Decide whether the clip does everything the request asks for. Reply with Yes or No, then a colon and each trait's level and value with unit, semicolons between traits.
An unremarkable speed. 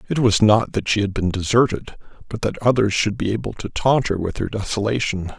No: fast, 225 wpm